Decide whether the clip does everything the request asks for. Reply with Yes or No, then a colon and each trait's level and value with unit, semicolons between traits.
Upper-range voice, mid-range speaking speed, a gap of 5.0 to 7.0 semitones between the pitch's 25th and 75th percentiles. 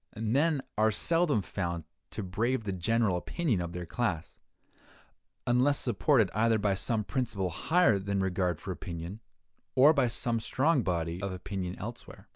No: low, 105 Hz; average, 150 wpm; average, 5.3 semitones